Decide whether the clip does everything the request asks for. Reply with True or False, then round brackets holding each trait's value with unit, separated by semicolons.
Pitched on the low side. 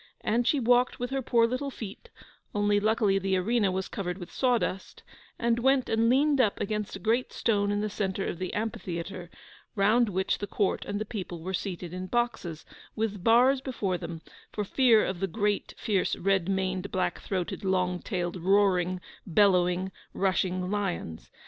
False (200 Hz)